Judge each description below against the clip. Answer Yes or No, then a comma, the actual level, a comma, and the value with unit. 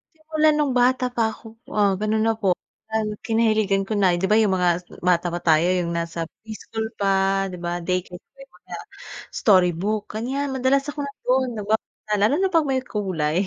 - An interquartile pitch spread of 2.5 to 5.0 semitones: No, wide, 5.6 semitones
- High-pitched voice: Yes, high, 215 Hz